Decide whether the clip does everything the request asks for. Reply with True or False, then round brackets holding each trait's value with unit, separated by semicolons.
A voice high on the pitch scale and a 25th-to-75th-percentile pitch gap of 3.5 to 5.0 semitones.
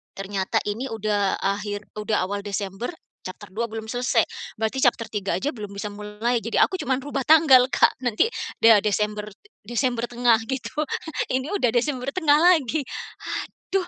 True (230 Hz; 4.0 semitones)